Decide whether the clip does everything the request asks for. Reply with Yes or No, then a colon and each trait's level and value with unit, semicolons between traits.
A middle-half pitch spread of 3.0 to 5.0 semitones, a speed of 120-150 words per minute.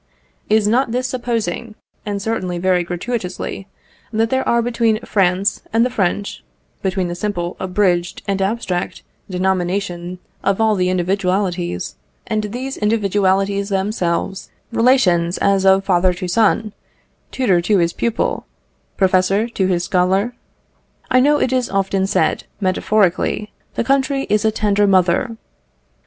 Yes: average, 3.5 semitones; slow, 135 wpm